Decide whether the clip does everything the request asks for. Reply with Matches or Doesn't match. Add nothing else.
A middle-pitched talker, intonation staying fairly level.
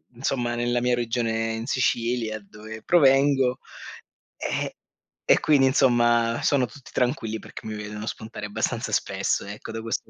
Doesn't match